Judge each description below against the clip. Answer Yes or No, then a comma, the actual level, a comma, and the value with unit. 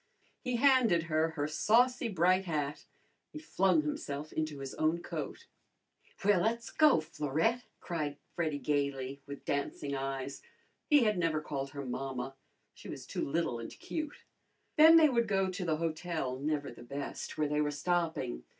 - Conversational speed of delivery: Yes, average, 160 wpm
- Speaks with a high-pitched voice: No, medium, 155 Hz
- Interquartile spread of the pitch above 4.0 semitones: Yes, average, 5.3 semitones